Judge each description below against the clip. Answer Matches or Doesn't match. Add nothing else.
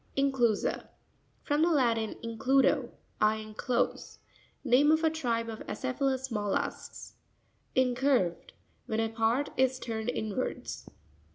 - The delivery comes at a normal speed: Doesn't match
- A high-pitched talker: Matches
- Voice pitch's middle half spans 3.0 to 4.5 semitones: Matches